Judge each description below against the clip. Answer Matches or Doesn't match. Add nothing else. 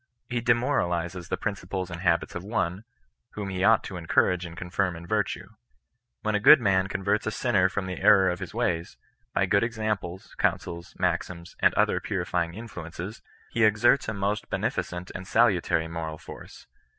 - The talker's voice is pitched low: Matches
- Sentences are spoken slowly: Doesn't match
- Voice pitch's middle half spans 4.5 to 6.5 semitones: Doesn't match